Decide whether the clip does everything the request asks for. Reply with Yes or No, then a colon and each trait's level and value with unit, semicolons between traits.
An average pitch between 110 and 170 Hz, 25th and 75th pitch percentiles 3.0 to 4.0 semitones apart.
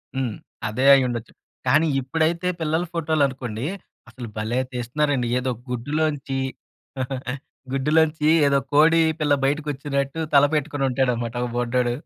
Yes: low, 135 Hz; average, 3.5 semitones